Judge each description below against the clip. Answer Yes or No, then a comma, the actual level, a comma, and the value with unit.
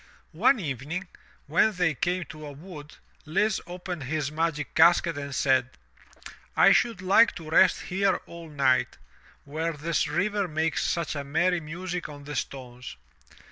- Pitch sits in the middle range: Yes, medium, 160 Hz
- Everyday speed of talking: Yes, average, 150 wpm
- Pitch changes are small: No, average, 3.7 semitones